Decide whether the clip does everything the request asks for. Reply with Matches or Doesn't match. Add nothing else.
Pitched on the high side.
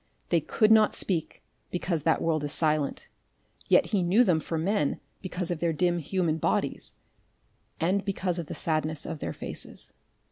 Doesn't match